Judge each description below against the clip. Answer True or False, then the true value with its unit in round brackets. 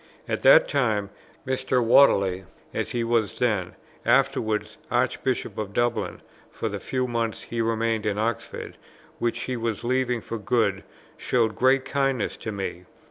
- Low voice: True (115 Hz)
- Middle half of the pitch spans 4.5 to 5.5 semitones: False (2.9 semitones)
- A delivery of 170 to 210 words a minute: False (145 wpm)